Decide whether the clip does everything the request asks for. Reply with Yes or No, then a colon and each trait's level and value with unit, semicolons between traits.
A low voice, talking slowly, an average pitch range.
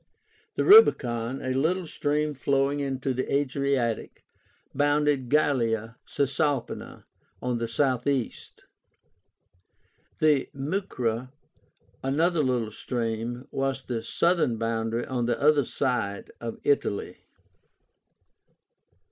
Yes: low, 130 Hz; slow, 95 wpm; average, 3.5 semitones